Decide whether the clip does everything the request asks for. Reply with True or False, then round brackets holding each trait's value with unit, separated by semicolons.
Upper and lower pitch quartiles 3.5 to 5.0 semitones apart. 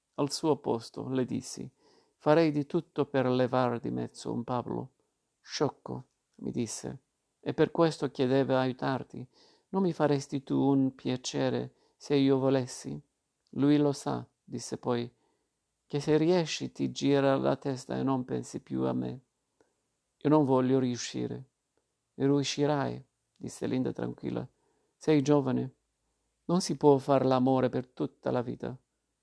False (3.1 semitones)